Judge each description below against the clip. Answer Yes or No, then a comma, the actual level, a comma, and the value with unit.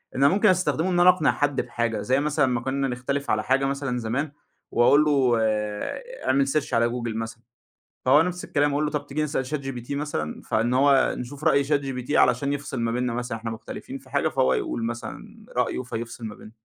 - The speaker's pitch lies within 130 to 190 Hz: Yes, low, 135 Hz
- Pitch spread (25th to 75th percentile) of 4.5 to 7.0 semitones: No, average, 3.4 semitones